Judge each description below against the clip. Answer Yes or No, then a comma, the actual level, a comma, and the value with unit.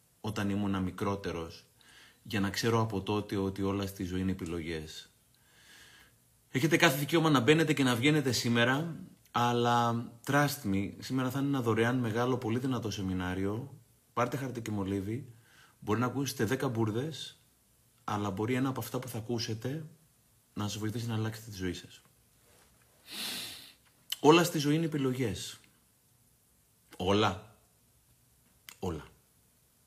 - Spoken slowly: No, average, 135 wpm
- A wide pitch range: No, average, 4.4 semitones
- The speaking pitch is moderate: No, low, 120 Hz